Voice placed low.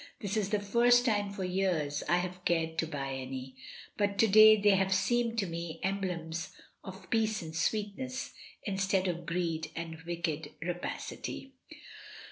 No: medium, 185 Hz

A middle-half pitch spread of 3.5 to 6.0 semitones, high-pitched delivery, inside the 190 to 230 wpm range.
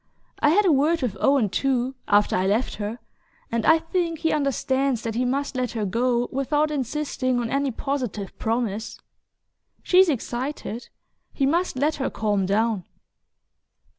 No: average, 4.3 semitones; very high, 255 Hz; average, 155 wpm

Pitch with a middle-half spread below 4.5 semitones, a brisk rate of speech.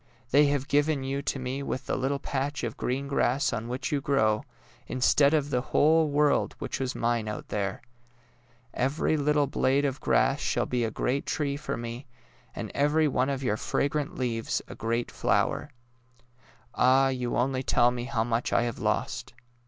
No: average, 2.8 semitones; average, 185 wpm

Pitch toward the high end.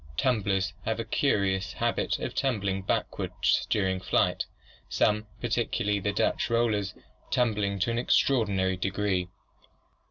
No: low, 100 Hz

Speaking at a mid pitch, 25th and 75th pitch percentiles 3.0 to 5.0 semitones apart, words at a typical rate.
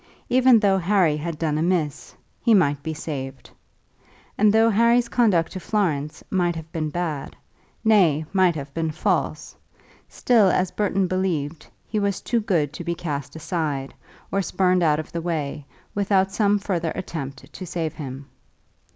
Yes: medium, 170 Hz; average, 4.5 semitones; average, 160 wpm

